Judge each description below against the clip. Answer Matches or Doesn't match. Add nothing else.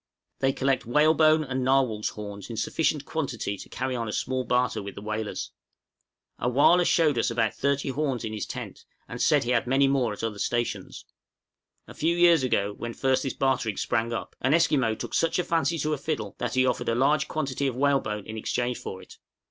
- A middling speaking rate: Doesn't match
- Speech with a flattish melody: Doesn't match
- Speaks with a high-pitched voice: Doesn't match